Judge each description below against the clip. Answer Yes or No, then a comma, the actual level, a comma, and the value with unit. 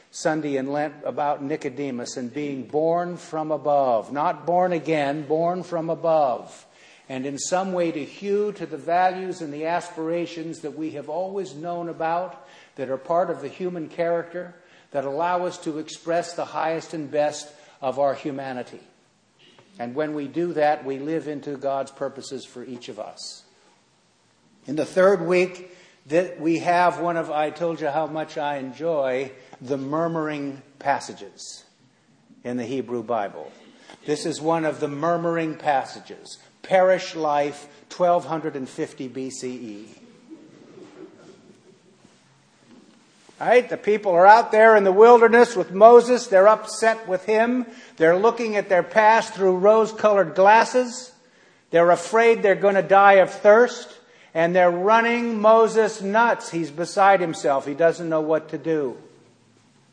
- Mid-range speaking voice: Yes, medium, 165 Hz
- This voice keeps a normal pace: Yes, average, 150 wpm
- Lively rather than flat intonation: No, average, 4.0 semitones